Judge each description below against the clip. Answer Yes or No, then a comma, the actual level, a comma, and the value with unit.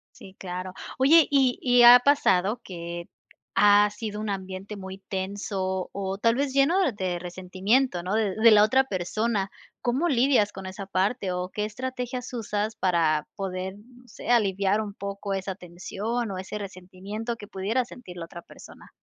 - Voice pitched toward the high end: Yes, high, 205 Hz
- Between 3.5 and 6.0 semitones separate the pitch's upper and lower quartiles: Yes, average, 4.1 semitones